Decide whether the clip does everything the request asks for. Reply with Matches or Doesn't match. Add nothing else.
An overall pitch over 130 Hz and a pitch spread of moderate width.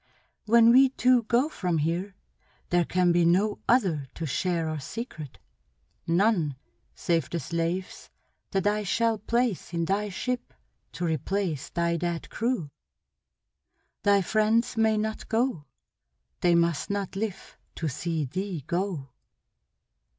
Matches